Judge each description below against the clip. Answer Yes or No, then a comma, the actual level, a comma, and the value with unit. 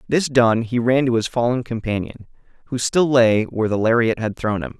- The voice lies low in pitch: Yes, low, 120 Hz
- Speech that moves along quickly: Yes, fast, 215 wpm